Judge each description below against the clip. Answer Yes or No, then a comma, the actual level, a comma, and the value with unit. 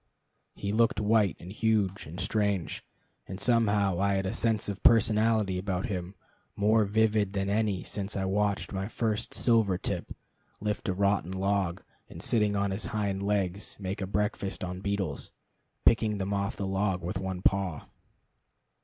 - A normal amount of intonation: No, narrow, 1.7 semitones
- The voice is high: No, low, 100 Hz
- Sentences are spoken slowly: No, average, 160 wpm